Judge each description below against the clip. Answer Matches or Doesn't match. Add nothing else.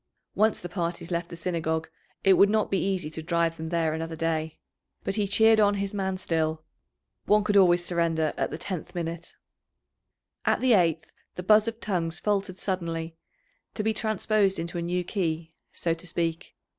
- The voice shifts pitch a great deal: Doesn't match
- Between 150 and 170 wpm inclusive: Doesn't match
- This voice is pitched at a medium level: Matches